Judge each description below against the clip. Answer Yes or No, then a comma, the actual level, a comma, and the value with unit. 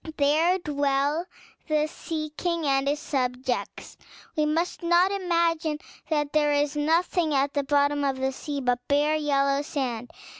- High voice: Yes, very high, 295 Hz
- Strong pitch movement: No, narrow, 2.5 semitones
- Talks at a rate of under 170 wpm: Yes, average, 150 wpm